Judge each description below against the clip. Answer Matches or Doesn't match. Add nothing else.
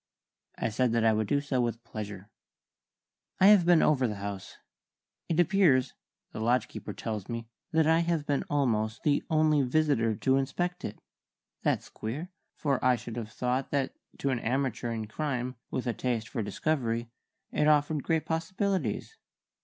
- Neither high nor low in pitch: Doesn't match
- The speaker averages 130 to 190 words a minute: Matches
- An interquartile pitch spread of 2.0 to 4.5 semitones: Doesn't match